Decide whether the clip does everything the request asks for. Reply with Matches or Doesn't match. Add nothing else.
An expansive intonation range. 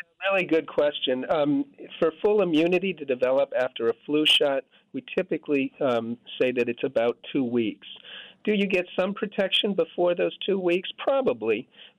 Matches